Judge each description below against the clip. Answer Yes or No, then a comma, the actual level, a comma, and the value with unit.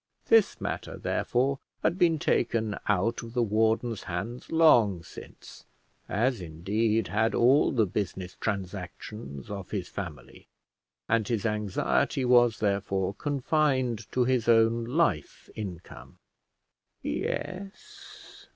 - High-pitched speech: No, low, 110 Hz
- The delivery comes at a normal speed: No, slow, 115 wpm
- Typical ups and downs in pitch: Yes, average, 4.2 semitones